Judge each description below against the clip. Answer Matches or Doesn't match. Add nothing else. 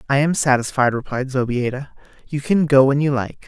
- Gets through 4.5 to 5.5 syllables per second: Matches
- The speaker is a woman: Doesn't match